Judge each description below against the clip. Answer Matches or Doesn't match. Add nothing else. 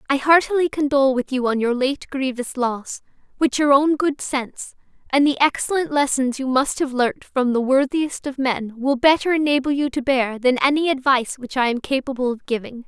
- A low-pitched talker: Doesn't match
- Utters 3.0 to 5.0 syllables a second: Doesn't match